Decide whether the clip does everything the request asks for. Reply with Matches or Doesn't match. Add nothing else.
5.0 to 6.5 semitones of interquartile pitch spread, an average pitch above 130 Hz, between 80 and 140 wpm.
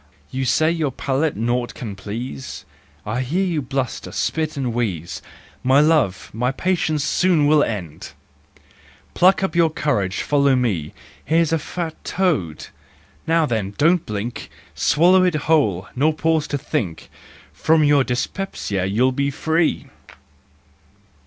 Matches